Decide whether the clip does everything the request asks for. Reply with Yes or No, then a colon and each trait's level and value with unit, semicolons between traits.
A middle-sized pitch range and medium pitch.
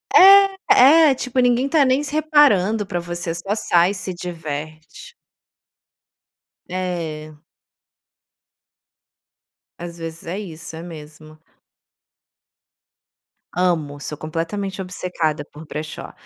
No: wide, 7.1 semitones; medium, 175 Hz